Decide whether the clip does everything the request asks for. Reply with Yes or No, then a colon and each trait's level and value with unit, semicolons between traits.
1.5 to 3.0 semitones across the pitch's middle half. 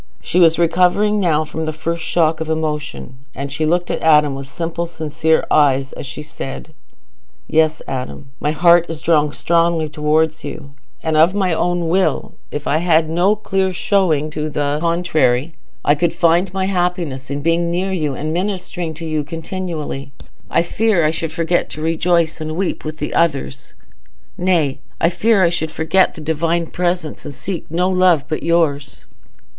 Yes: narrow, 2.4 semitones